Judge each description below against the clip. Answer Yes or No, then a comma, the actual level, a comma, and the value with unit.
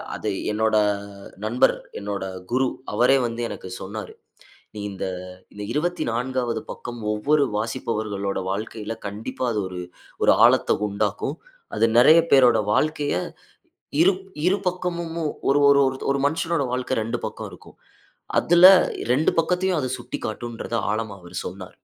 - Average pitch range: No, wide, 5.7 semitones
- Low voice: Yes, low, 120 Hz